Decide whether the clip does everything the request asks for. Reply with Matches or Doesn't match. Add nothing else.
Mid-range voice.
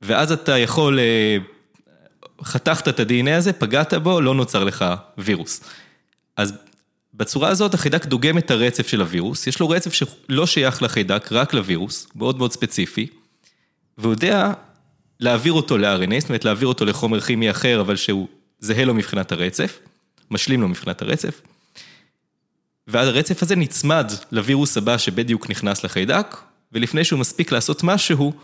Doesn't match